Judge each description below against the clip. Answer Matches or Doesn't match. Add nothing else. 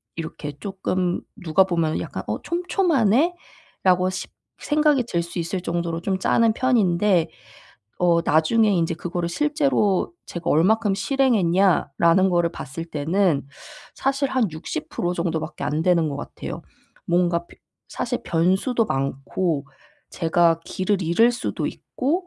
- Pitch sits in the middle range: Matches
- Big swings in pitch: Doesn't match